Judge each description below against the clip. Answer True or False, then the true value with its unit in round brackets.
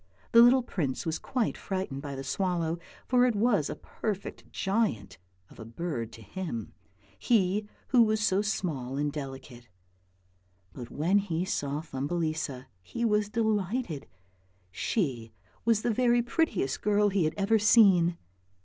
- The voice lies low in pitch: False (185 Hz)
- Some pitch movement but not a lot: False (7.3 semitones)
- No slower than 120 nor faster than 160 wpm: True (145 wpm)